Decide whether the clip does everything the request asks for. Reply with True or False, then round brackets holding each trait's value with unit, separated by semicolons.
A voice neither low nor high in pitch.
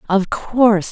False (210 Hz)